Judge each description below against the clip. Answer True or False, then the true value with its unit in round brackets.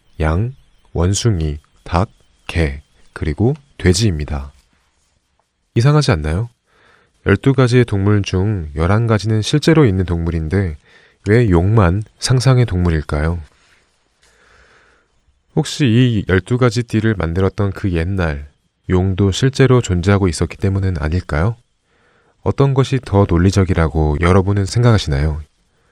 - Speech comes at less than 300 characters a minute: True (240 characters per minute)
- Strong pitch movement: True (5.8 semitones)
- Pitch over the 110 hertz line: False (95 Hz)